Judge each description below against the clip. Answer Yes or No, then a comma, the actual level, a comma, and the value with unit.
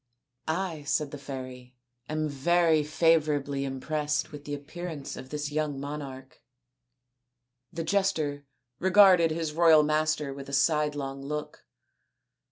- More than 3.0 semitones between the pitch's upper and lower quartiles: No, narrow, 2.4 semitones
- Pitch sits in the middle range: Yes, medium, 150 Hz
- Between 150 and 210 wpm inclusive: No, slow, 135 wpm